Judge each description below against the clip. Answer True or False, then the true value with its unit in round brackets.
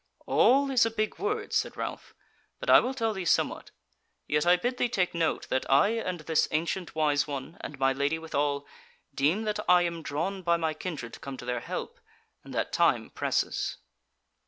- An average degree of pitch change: False (6.7 semitones)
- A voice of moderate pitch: True (170 Hz)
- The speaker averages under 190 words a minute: False (195 wpm)